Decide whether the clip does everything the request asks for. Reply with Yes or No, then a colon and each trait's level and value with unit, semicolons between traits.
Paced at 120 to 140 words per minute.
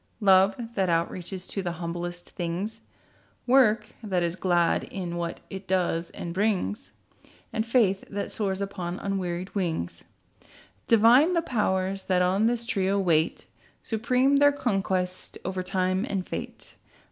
Yes: slow, 135 wpm